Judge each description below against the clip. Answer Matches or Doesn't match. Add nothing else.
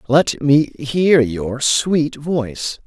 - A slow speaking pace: Matches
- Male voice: Matches